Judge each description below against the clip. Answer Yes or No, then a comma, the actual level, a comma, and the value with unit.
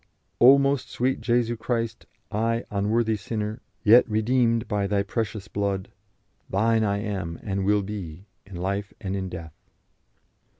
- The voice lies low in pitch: Yes, low, 105 Hz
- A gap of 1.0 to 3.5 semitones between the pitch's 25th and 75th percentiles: Yes, average, 2.7 semitones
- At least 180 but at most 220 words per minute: No, average, 140 wpm